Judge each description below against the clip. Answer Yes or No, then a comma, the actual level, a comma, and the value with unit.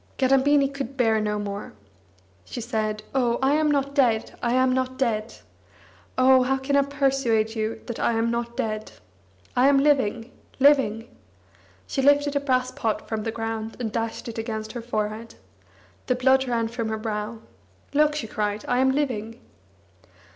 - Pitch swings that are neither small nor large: Yes, average, 3.3 semitones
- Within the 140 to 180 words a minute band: Yes, average, 170 wpm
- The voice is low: No, high, 240 Hz